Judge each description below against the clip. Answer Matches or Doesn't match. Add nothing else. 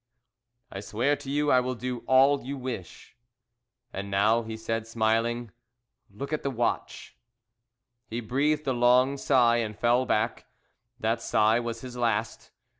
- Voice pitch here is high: Doesn't match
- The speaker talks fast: Doesn't match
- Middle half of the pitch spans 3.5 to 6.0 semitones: Doesn't match